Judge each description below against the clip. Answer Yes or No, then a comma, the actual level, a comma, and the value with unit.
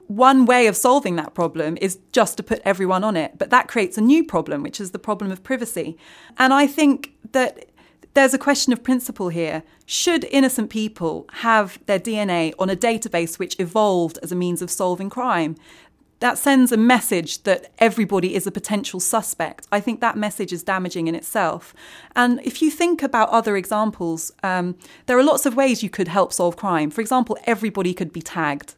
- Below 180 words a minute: No, average, 195 wpm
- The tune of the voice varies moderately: No, wide, 5.7 semitones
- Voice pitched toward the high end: Yes, high, 215 Hz